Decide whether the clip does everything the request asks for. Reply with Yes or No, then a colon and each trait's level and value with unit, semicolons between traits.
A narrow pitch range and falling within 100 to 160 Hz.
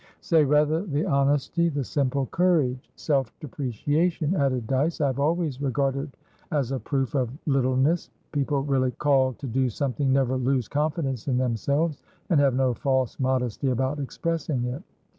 Yes: narrow, 2.3 semitones; medium, 140 Hz